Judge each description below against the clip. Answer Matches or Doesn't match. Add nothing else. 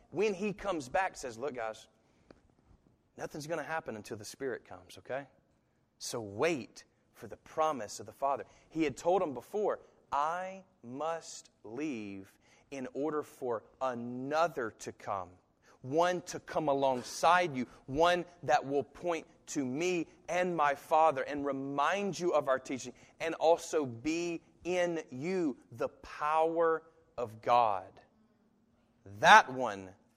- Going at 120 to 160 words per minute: Matches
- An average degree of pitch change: Matches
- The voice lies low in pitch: Doesn't match